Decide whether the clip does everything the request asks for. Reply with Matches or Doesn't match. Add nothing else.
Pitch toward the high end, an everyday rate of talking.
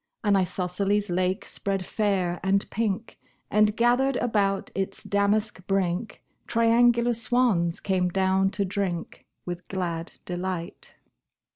Doesn't match